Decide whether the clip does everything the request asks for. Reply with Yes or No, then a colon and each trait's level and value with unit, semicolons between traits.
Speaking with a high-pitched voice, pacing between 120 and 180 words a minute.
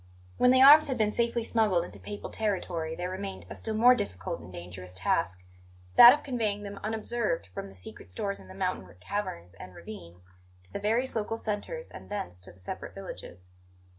No: high, 195 Hz; average, 195 wpm